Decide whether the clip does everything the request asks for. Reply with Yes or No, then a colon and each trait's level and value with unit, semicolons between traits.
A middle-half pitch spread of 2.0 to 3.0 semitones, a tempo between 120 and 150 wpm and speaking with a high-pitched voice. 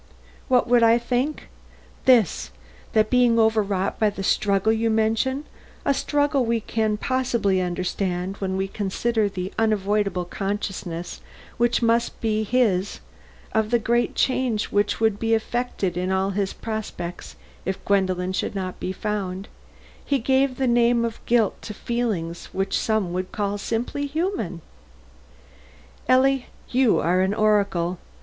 No: average, 3.8 semitones; average, 140 wpm; high, 215 Hz